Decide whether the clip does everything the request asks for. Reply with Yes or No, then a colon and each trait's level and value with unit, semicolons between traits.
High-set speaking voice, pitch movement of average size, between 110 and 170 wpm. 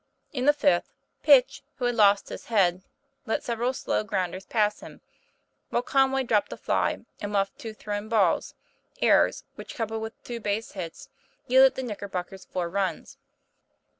Yes: high, 215 Hz; average, 3.6 semitones; average, 165 wpm